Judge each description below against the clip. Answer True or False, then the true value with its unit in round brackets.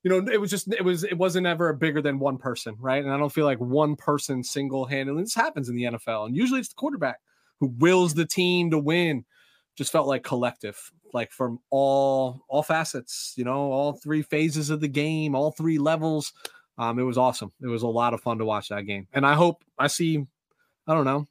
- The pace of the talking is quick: True (230 wpm)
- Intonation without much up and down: False (3.8 semitones)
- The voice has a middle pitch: True (145 Hz)